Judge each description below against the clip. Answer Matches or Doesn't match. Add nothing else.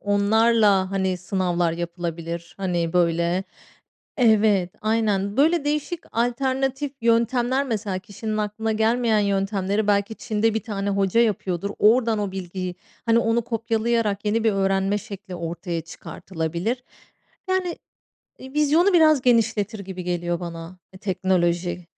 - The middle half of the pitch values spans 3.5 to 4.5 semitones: Matches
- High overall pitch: Matches